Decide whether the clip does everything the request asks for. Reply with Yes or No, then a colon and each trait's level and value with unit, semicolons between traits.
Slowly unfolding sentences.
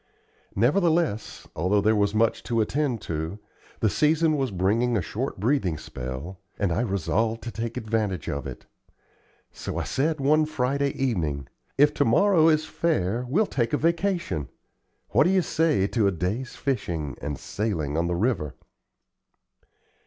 No: average, 155 wpm